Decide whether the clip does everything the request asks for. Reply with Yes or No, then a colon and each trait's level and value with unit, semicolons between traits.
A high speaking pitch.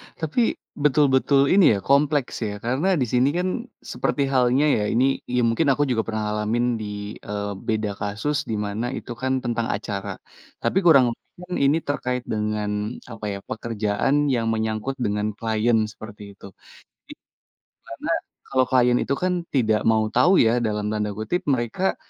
No: low, 120 Hz